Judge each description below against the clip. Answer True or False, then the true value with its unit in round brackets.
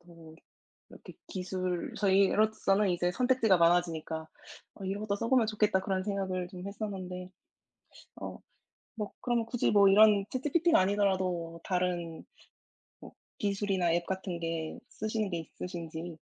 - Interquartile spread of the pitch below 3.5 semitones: True (3.0 semitones)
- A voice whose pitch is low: False (190 Hz)